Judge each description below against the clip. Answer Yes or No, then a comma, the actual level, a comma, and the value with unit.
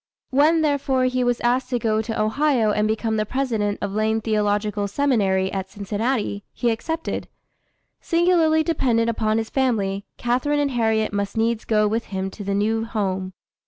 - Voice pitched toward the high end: Yes, high, 225 Hz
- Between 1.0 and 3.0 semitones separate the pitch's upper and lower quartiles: No, average, 3.7 semitones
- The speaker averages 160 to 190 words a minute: Yes, average, 165 wpm